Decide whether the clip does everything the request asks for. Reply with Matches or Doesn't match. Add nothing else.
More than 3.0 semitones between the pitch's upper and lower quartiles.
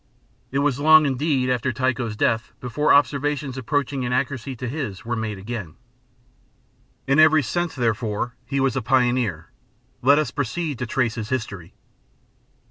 Matches